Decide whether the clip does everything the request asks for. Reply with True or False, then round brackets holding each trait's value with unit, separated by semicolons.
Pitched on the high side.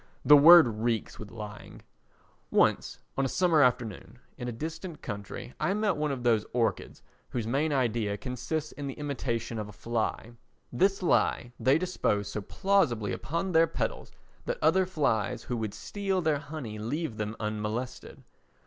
False (125 Hz)